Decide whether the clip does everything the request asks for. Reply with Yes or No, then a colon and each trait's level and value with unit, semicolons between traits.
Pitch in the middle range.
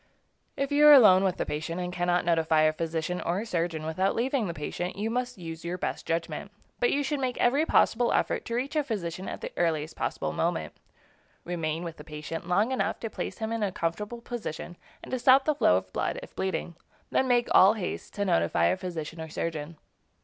Yes: medium, 180 Hz